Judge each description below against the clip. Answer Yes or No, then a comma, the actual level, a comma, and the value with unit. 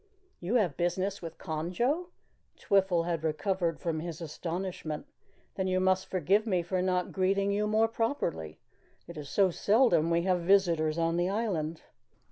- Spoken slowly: No, average, 160 wpm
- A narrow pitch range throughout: No, average, 3.1 semitones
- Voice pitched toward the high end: No, medium, 180 Hz